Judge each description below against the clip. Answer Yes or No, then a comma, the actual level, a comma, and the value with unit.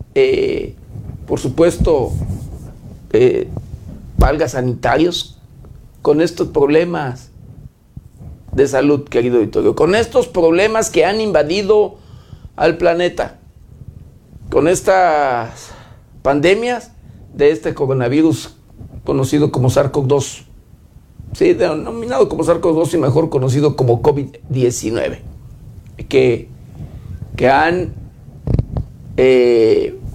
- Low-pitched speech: No, medium, 145 Hz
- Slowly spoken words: Yes, slow, 85 wpm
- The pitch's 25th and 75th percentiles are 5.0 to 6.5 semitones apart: Yes, wide, 5.5 semitones